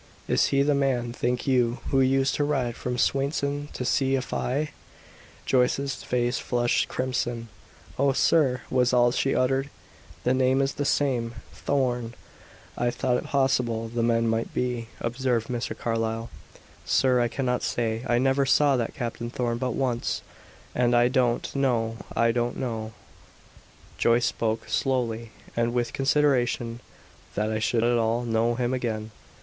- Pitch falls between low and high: No, low, 125 Hz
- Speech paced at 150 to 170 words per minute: Yes, average, 155 wpm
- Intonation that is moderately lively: No, narrow, 2.2 semitones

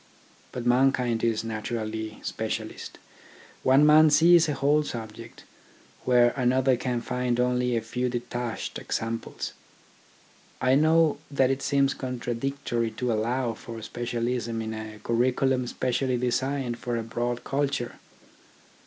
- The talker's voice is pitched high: No, low, 125 Hz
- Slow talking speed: Yes, slow, 130 wpm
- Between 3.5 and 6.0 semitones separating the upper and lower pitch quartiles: No, narrow, 2.4 semitones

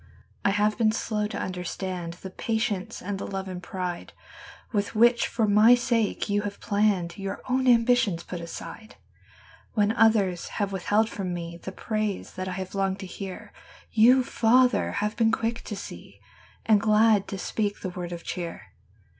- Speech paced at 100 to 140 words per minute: No, average, 155 wpm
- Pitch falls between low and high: No, high, 205 Hz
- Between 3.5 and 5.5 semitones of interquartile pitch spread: No, average, 3.0 semitones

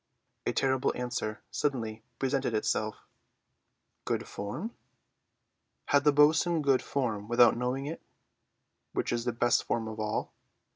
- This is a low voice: Yes, low, 125 Hz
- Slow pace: Yes, slow, 125 wpm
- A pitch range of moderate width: Yes, average, 4.0 semitones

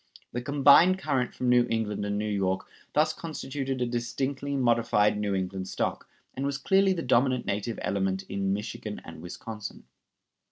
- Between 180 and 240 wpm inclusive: No, average, 160 wpm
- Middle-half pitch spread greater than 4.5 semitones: Yes, average, 5.2 semitones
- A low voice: Yes, low, 120 Hz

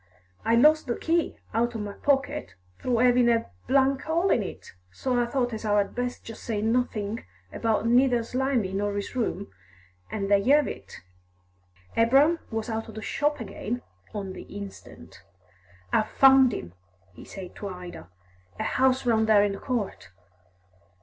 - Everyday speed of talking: Yes, average, 165 wpm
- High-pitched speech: Yes, high, 230 Hz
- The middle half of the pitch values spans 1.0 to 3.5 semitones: No, average, 4.2 semitones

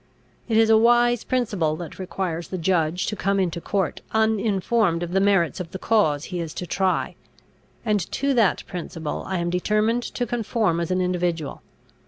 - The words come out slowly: No, average, 180 wpm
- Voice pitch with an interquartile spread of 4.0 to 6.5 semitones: Yes, average, 4.3 semitones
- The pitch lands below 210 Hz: Yes, high, 190 Hz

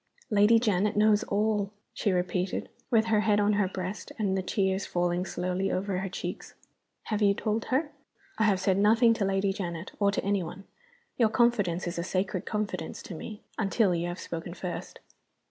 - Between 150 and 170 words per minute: No, average, 185 wpm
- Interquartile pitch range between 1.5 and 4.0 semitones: Yes, narrow, 2.5 semitones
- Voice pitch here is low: No, high, 200 Hz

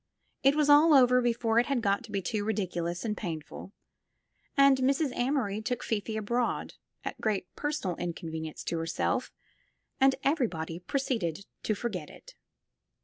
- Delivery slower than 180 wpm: Yes, average, 145 wpm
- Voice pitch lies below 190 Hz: No, high, 220 Hz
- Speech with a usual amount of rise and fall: No, wide, 6.4 semitones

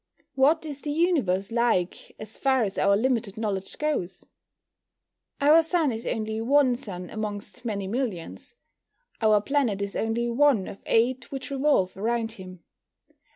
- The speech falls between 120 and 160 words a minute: Yes, average, 145 wpm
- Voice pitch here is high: Yes, high, 225 Hz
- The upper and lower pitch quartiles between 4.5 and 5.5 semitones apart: Yes, average, 5.2 semitones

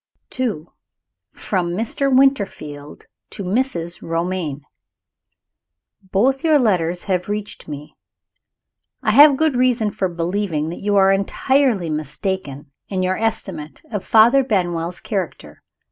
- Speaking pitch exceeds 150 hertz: Yes, high, 190 Hz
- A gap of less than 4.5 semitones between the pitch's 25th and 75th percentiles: No, average, 5.3 semitones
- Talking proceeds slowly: Yes, slow, 115 wpm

